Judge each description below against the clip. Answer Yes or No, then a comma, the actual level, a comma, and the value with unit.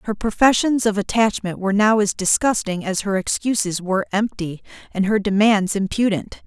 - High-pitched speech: Yes, high, 205 Hz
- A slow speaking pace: No, average, 160 wpm